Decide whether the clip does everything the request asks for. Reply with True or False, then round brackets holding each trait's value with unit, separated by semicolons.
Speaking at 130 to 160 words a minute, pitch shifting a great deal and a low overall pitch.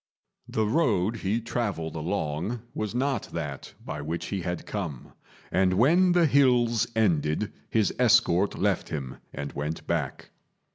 True (140 wpm; 6.5 semitones; 100 Hz)